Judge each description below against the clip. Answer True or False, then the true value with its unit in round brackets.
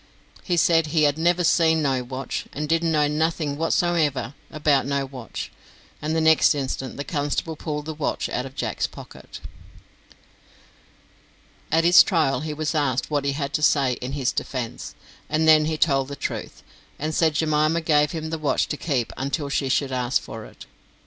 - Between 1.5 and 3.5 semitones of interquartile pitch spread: True (2.4 semitones)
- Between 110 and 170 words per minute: False (180 wpm)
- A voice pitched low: False (150 Hz)